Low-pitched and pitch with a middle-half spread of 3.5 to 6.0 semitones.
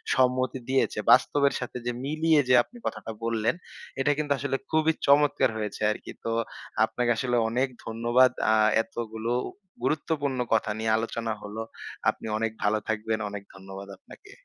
Yes: low, 120 Hz; average, 4.0 semitones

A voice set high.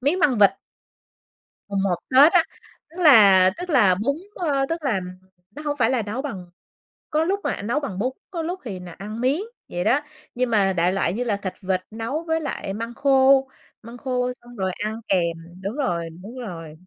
Yes: high, 235 Hz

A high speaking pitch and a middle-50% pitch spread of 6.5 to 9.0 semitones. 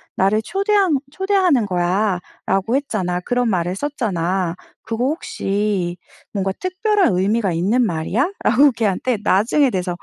Yes: high, 215 Hz; wide, 7.1 semitones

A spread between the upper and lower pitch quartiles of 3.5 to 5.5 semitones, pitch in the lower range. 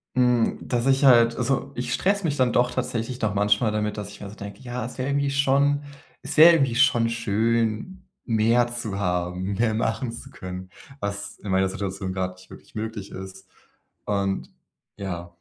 Yes: average, 4.1 semitones; low, 115 Hz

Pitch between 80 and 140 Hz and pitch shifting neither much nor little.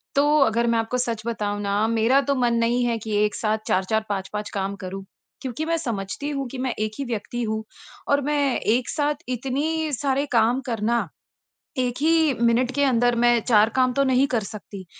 No: high, 235 Hz; average, 3.7 semitones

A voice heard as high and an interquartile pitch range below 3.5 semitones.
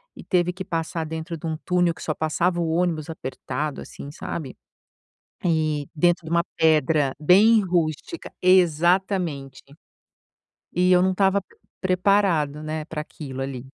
No: medium, 165 Hz; average, 2.9 semitones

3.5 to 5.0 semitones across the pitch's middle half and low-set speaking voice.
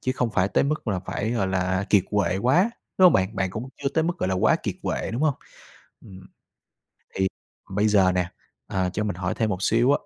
Yes: average, 4.7 semitones; low, 100 Hz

